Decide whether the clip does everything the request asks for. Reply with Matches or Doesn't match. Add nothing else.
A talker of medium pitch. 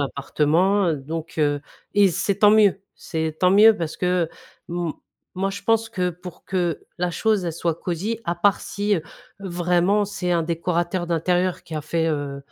Matches